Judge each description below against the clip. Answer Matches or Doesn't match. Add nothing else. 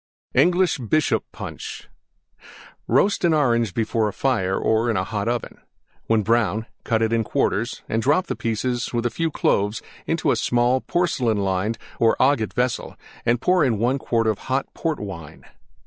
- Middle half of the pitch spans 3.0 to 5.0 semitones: Matches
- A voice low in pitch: Matches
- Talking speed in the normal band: Matches